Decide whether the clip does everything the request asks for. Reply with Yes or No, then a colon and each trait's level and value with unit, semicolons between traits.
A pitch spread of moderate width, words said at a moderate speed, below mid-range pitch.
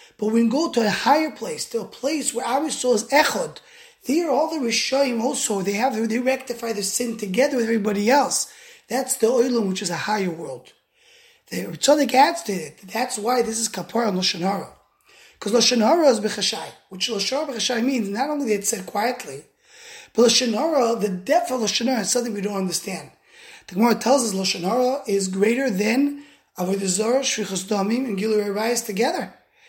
No: average, 4.6 semitones; average, 185 wpm; high, 235 Hz